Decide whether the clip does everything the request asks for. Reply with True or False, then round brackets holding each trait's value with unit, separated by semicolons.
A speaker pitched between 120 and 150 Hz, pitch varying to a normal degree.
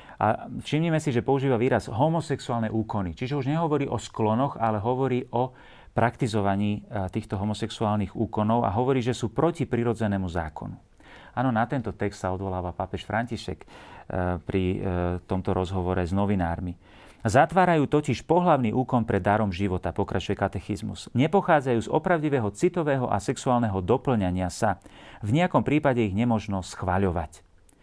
False (110 Hz; 5.0 semitones)